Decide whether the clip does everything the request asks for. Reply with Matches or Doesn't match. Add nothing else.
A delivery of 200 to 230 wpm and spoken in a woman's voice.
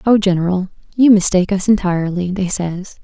Doesn't match